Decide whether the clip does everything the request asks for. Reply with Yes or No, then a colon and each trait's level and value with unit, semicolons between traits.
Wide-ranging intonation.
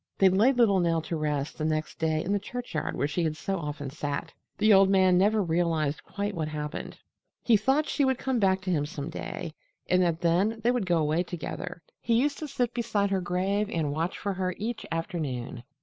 No: average, 4.7 semitones